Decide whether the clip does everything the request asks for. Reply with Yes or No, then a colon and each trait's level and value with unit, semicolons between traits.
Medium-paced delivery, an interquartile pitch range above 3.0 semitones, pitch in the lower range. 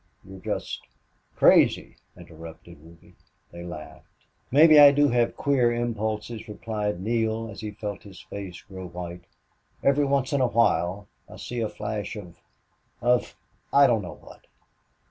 Yes: average, 150 wpm; average, 4.7 semitones; low, 105 Hz